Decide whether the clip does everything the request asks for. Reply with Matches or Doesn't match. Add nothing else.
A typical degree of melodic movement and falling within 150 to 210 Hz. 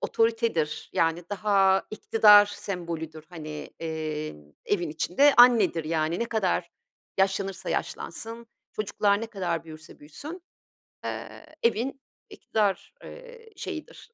Doesn't match